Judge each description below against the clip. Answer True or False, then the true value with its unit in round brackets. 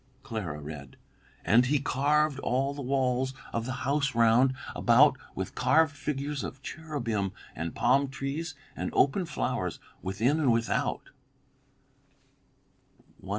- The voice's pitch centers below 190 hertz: True (135 Hz)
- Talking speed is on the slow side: True (120 wpm)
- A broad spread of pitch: False (3.7 semitones)